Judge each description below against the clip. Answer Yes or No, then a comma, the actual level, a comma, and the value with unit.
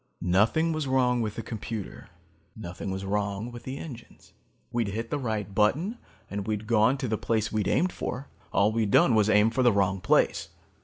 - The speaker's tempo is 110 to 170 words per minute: No, average, 195 wpm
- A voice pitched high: No, low, 110 Hz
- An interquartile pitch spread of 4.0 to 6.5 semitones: No, average, 3.4 semitones